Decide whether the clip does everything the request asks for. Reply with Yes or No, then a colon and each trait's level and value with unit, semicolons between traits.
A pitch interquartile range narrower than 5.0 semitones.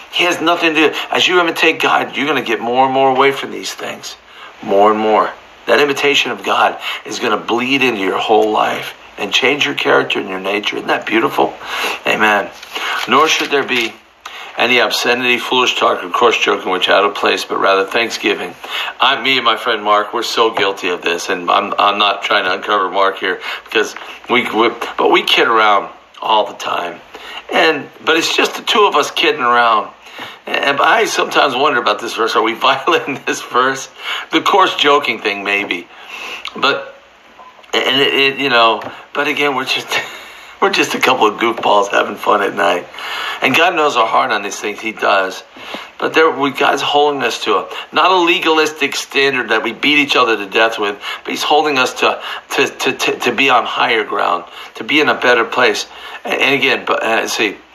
No: wide, 5.5 semitones